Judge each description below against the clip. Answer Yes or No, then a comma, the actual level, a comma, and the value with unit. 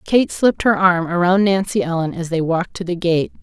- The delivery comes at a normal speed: No, fast, 230 wpm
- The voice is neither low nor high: Yes, medium, 180 Hz